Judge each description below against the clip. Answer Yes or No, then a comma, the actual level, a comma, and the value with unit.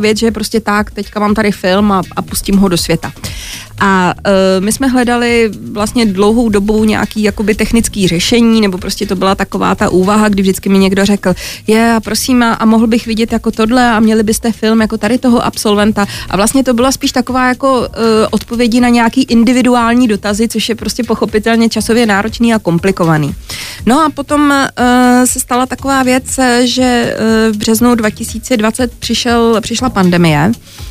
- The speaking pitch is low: No, high, 220 Hz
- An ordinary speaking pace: No, fast, 175 wpm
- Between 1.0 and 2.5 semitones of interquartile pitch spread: No, average, 2.9 semitones